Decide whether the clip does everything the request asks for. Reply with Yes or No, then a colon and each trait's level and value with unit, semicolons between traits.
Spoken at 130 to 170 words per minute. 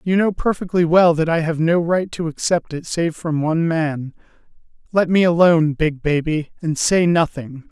No: average, 185 wpm